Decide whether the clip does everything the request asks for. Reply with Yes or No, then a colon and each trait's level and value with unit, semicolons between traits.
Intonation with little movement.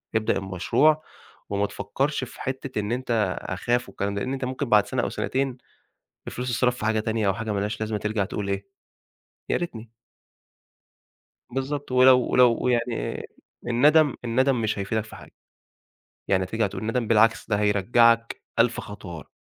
No: average, 3.6 semitones